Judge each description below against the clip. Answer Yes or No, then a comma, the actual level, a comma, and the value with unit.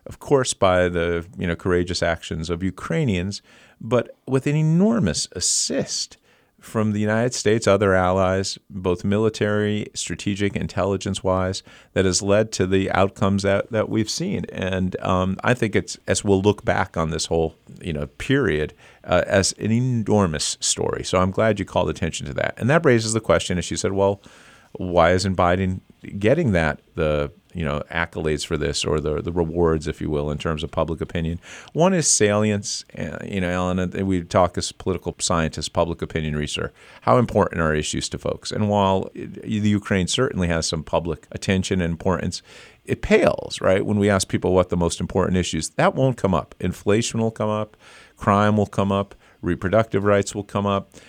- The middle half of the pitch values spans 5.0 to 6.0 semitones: No, average, 3.4 semitones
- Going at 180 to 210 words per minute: Yes, average, 185 wpm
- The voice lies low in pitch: Yes, very low, 95 Hz